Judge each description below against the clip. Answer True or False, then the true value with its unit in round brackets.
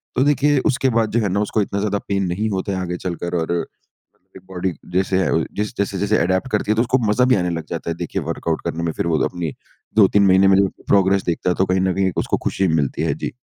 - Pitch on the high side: False (95 Hz)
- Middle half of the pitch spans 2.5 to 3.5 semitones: True (2.9 semitones)